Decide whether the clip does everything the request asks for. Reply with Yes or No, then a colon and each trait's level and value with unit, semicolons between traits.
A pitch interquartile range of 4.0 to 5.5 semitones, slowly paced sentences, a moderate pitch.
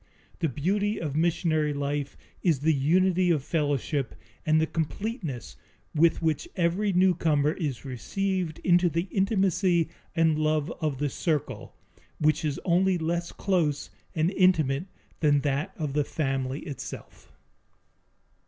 No: average, 3.5 semitones; slow, 130 wpm; medium, 160 Hz